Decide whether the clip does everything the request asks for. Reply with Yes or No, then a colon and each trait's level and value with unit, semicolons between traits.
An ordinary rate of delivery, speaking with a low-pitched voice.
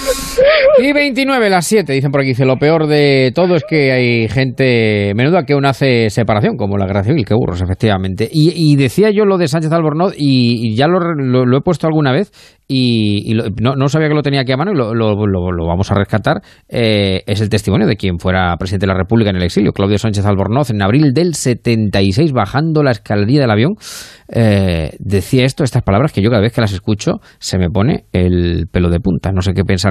No: fast, 230 wpm; low, 120 Hz